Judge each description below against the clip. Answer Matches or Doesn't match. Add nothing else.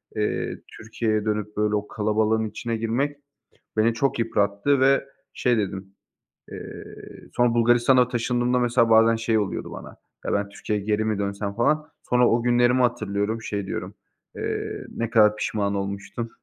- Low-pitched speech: Matches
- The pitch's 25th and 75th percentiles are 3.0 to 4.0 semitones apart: Doesn't match